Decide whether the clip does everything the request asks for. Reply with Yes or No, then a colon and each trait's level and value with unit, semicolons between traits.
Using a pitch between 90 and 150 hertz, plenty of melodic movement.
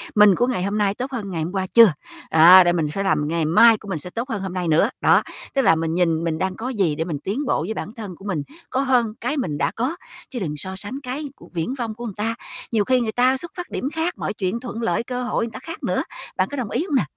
No: high, 210 Hz; wide, 5.7 semitones